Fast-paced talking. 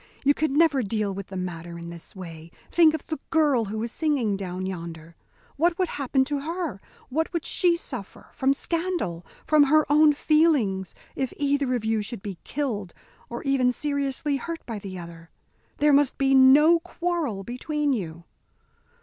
No: average, 175 wpm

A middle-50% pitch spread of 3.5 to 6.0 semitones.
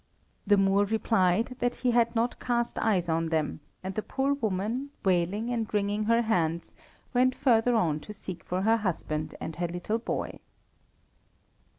Yes: average, 4.6 semitones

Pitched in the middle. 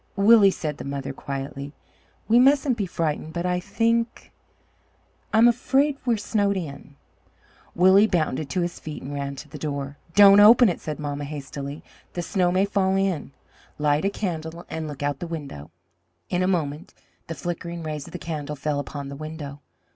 Yes: medium, 165 Hz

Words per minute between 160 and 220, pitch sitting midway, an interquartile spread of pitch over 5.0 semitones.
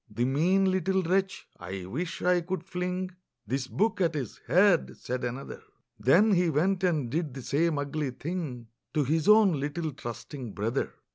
Yes: average, 165 wpm; medium, 160 Hz; wide, 5.5 semitones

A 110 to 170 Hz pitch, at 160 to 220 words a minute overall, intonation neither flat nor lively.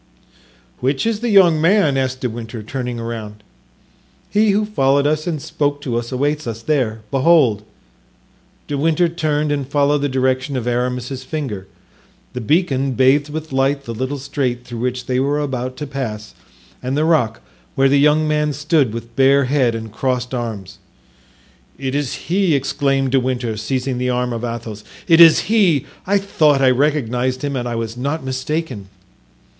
Yes: low, 135 Hz; average, 170 wpm; average, 3.4 semitones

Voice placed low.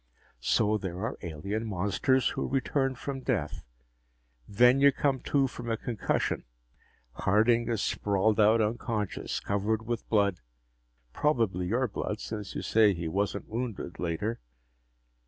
Yes: low, 110 Hz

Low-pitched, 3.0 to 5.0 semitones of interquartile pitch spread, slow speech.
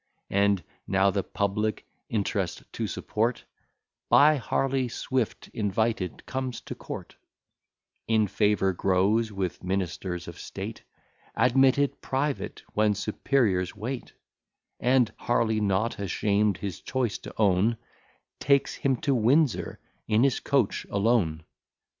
Yes: low, 110 Hz; average, 4.4 semitones; slow, 115 wpm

